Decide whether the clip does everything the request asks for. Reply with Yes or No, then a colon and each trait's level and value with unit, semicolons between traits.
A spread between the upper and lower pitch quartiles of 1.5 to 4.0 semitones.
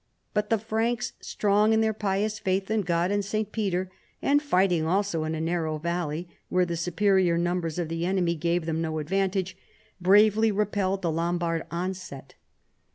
Yes: average, 3.3 semitones